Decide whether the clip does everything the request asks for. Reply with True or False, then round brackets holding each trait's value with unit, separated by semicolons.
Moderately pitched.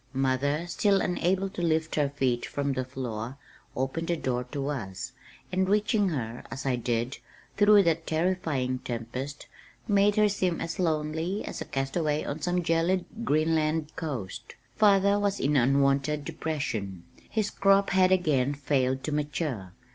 True (150 Hz)